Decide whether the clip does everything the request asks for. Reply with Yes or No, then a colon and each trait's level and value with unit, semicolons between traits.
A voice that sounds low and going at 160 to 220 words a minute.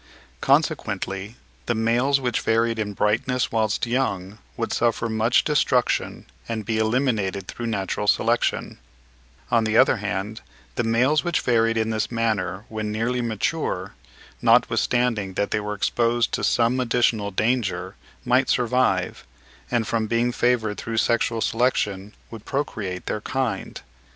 No: low, 115 Hz; slow, 135 wpm